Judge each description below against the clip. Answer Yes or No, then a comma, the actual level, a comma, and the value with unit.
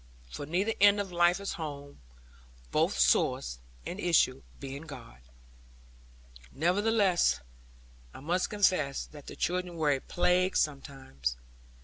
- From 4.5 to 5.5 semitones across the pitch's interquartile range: Yes, average, 4.8 semitones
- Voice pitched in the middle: Yes, medium, 165 Hz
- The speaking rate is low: Yes, slow, 120 wpm